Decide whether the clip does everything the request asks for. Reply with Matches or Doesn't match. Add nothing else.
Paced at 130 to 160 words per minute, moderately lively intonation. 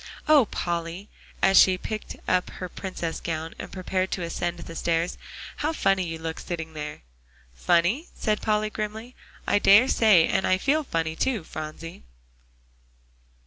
Matches